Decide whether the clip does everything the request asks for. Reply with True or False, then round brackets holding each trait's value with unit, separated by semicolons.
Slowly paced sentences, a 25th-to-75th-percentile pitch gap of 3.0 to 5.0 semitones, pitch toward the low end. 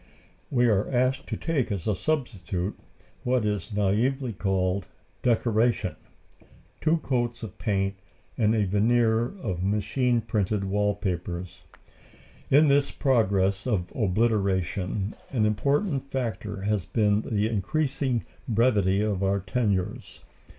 True (120 wpm; 4.0 semitones; 105 Hz)